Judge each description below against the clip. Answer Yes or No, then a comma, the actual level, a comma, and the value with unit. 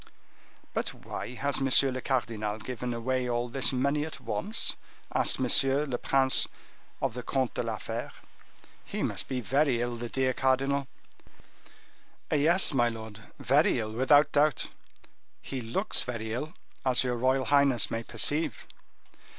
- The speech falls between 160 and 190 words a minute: No, average, 150 wpm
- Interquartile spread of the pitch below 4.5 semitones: Yes, narrow, 2.6 semitones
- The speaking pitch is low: Yes, low, 130 Hz